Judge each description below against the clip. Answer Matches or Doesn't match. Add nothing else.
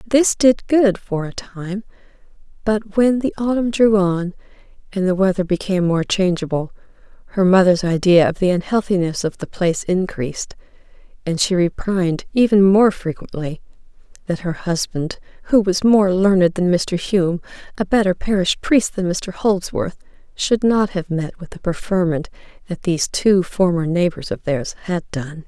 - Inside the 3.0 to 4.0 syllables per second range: Doesn't match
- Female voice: Matches